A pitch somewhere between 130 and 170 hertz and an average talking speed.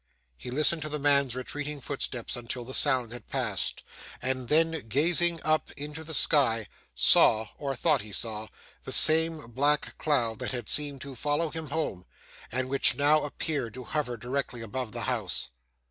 Yes: medium, 140 Hz; average, 170 wpm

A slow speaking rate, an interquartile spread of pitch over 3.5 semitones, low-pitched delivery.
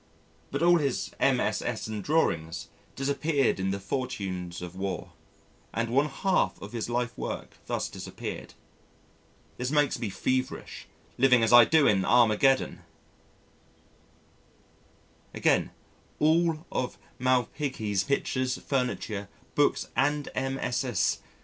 Yes: slow, 110 wpm; average, 5.1 semitones; low, 125 Hz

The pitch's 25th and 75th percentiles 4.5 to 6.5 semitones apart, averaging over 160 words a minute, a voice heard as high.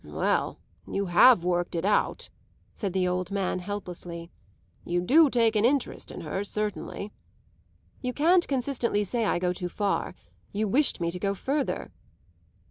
No: average, 5.1 semitones; average, 155 wpm; high, 200 Hz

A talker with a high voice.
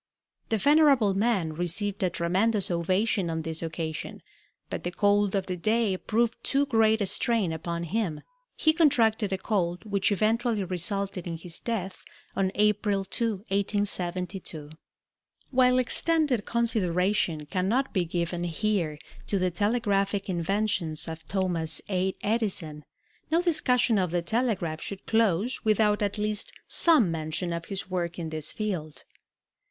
Yes: high, 195 Hz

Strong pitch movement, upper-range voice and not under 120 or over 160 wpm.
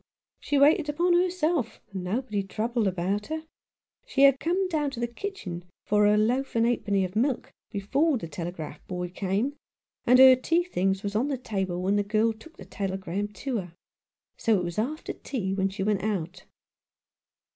No: wide, 6.2 semitones; high, 215 Hz; average, 180 wpm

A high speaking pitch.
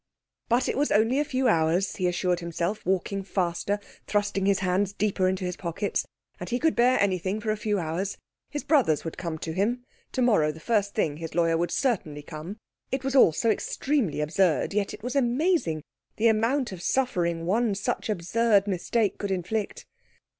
Yes: high, 200 Hz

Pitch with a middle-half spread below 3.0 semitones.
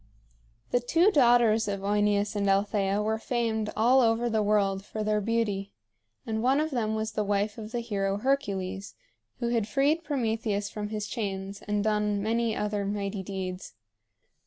Yes: narrow, 2.4 semitones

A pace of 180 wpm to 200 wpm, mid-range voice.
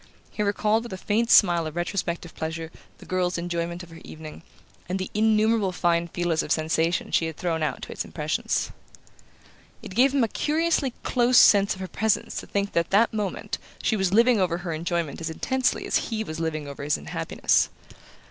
Yes: average, 195 wpm; medium, 180 Hz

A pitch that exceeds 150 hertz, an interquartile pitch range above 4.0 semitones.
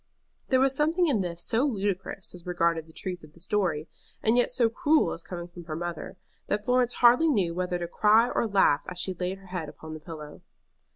Yes: medium, 185 Hz; wide, 5.6 semitones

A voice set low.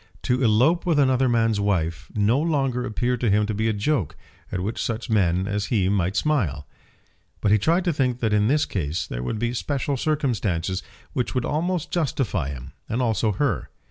Yes: low, 115 Hz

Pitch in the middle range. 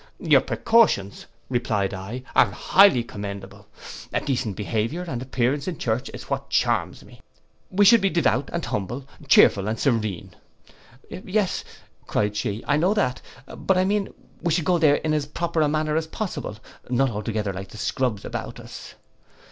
No: low, 130 Hz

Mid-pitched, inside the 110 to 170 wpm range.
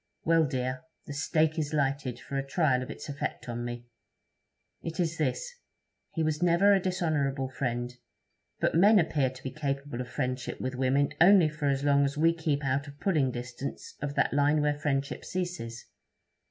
No: medium, 145 Hz; average, 180 wpm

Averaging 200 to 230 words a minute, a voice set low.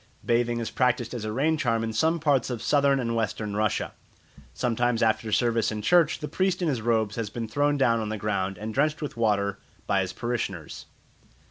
Yes: fast, 205 wpm; low, 115 Hz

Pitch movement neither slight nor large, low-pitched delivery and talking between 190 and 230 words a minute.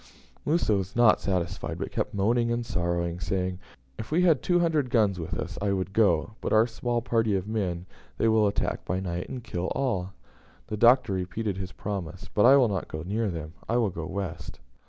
Yes: average, 4.5 semitones; low, 100 Hz; fast, 205 wpm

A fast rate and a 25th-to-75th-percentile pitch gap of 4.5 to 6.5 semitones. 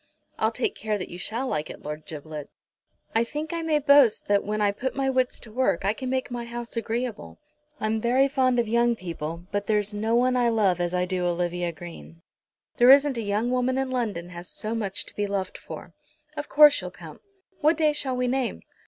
Yes: fast, 220 wpm; wide, 5.5 semitones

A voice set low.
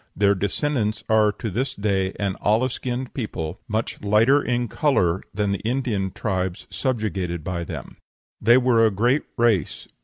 Yes: low, 105 Hz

